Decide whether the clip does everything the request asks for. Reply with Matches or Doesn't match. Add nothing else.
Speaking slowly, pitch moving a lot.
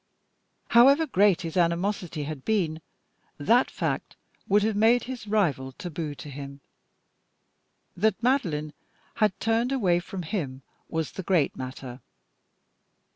Matches